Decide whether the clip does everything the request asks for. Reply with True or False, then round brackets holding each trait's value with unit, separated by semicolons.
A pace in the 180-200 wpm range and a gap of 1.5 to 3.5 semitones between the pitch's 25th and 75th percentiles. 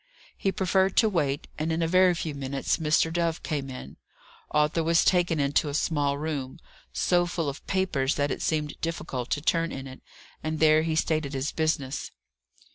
True (185 wpm; 2.9 semitones)